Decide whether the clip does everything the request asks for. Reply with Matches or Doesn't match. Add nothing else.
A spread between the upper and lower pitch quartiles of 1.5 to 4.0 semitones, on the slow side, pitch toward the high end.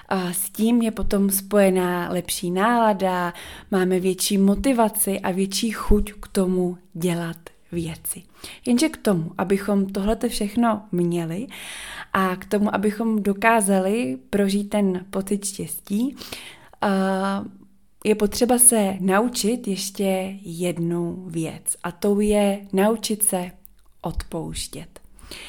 Matches